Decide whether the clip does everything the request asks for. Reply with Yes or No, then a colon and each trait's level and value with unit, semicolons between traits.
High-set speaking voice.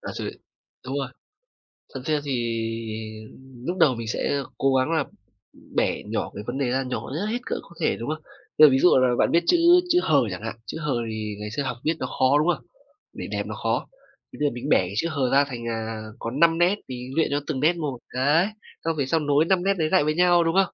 No: medium, 140 Hz